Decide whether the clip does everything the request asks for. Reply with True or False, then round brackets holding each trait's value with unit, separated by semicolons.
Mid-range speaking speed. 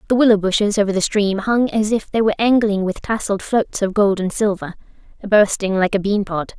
False (220 wpm)